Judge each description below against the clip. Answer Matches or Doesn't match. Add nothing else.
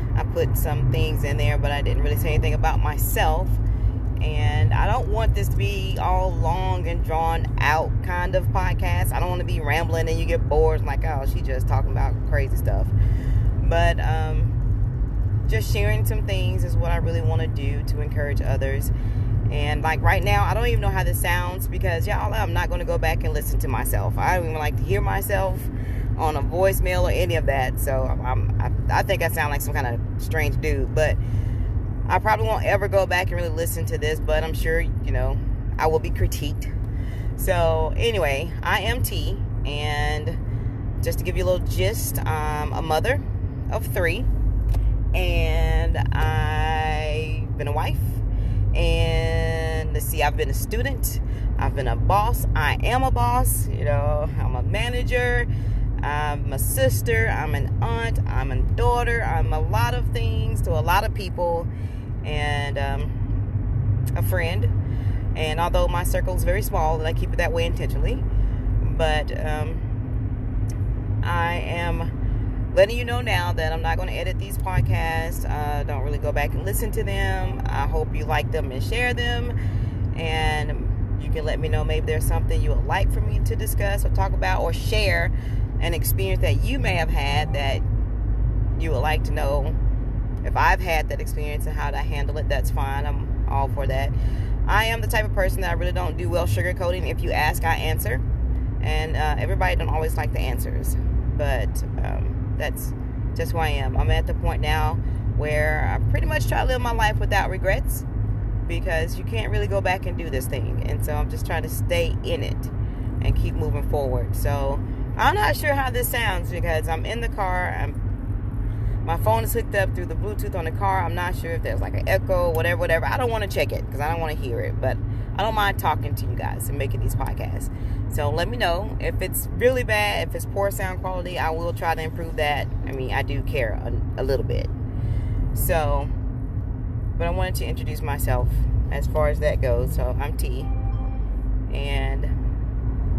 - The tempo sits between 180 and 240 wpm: Matches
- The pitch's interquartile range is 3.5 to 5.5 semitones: Doesn't match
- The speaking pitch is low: Matches